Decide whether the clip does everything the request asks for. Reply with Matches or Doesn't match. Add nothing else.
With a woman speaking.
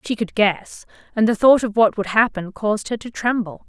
Matches